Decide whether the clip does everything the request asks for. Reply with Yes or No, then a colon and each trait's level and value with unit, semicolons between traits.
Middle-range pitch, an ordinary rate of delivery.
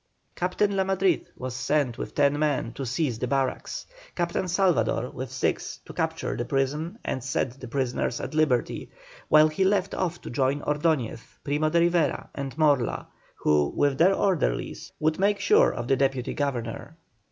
Yes: medium, 145 Hz; average, 170 wpm